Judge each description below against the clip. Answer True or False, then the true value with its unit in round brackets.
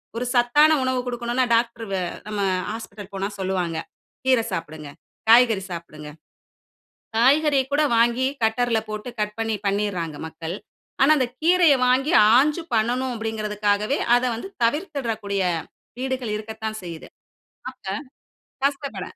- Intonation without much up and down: False (4.1 semitones)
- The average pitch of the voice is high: True (225 Hz)